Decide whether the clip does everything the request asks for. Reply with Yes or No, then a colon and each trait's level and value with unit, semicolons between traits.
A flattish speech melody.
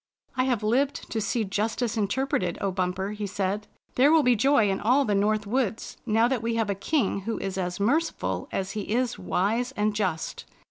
No: average, 3.9 semitones